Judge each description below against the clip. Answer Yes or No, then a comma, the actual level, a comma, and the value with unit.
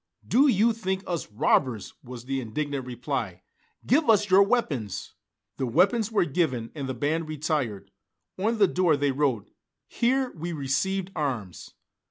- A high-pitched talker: No, medium, 150 Hz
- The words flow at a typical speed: Yes, average, 150 wpm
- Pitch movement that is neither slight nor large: No, wide, 7.4 semitones